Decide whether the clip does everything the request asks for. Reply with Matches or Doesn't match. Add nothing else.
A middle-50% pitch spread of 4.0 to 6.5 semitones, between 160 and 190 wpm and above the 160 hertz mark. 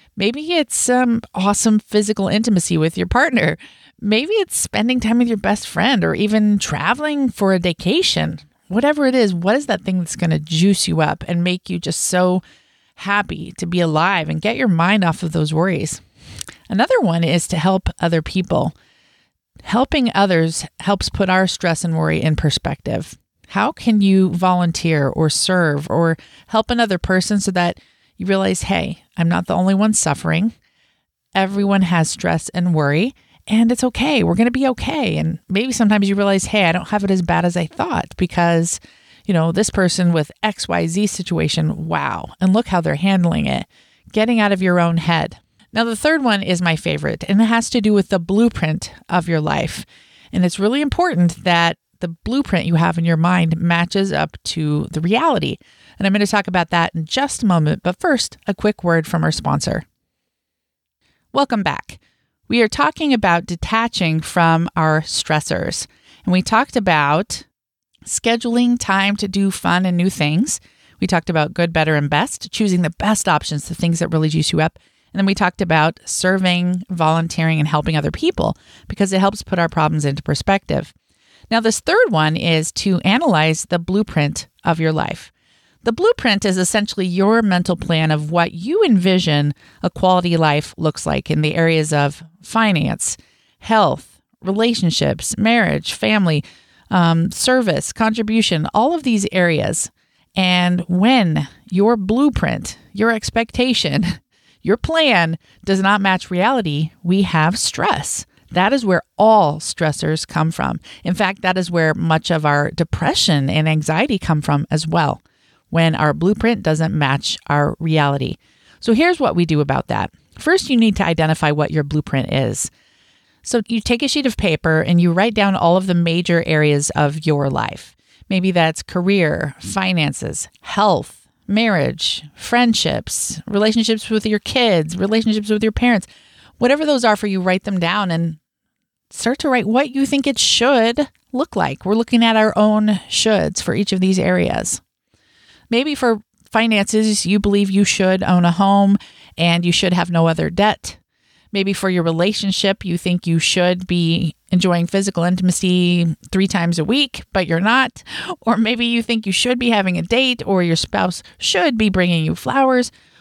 Matches